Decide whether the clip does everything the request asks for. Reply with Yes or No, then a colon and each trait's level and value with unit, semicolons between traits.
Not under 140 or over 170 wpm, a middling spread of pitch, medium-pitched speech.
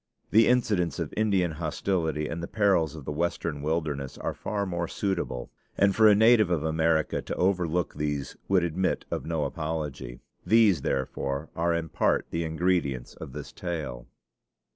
No: average, 165 wpm; average, 3.8 semitones; very low, 85 Hz